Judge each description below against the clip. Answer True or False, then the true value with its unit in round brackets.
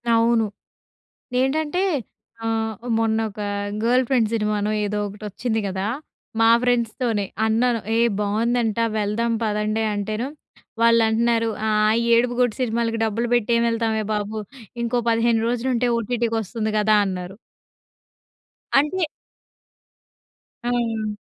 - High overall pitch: True (225 Hz)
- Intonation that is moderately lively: False (1.8 semitones)